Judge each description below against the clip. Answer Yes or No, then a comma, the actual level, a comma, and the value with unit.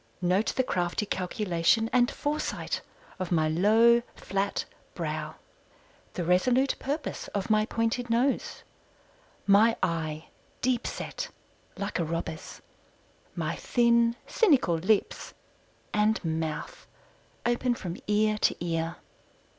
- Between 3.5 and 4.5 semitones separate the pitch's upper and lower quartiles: No, average, 5.3 semitones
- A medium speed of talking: No, slow, 110 wpm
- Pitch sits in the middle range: No, high, 210 Hz